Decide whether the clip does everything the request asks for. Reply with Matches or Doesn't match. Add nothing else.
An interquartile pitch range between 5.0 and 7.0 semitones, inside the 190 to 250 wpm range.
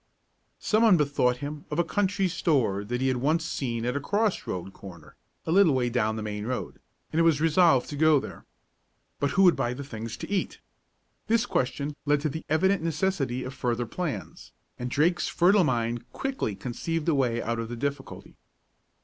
Matches